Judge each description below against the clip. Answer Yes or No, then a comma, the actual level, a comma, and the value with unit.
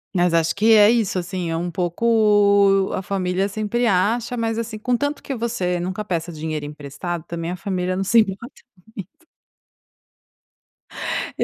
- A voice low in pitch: No, high, 195 Hz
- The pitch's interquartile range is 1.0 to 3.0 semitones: No, average, 4.2 semitones